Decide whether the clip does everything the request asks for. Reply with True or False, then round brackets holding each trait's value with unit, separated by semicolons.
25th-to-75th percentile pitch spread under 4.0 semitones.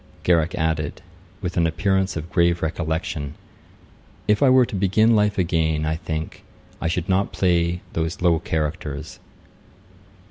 True (3.0 semitones)